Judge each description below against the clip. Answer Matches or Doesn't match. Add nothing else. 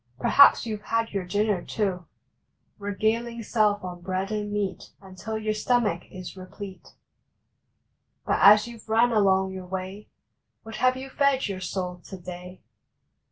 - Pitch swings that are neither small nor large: Matches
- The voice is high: Matches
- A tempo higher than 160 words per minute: Doesn't match